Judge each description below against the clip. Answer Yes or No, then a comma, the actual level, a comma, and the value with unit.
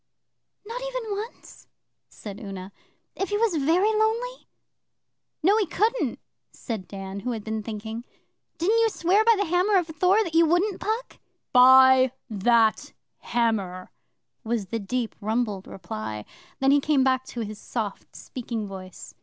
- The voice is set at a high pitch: Yes, very high, 260 Hz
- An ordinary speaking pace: Yes, average, 150 wpm